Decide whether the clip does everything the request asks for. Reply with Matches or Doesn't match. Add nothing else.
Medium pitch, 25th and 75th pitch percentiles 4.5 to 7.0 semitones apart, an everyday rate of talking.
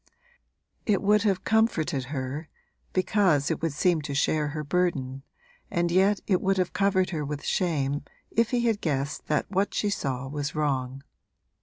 Matches